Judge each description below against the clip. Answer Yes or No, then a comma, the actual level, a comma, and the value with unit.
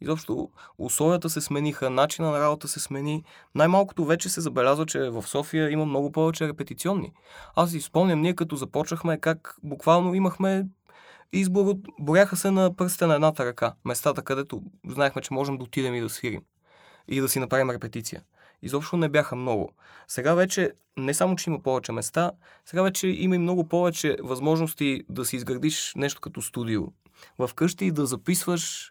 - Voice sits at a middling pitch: Yes, medium, 155 Hz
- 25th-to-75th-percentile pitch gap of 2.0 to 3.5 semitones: No, average, 4.2 semitones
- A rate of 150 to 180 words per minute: Yes, fast, 165 wpm